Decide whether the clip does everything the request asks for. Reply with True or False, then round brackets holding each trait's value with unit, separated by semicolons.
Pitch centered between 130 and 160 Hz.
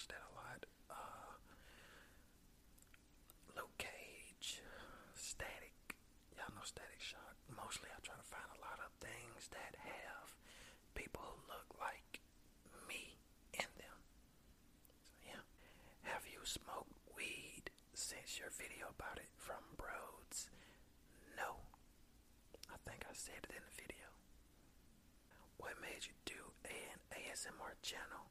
False (75 Hz)